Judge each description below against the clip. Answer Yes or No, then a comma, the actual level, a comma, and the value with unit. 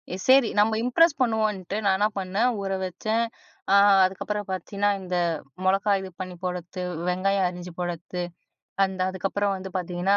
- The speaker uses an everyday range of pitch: No, narrow, 2.3 semitones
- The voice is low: No, high, 195 Hz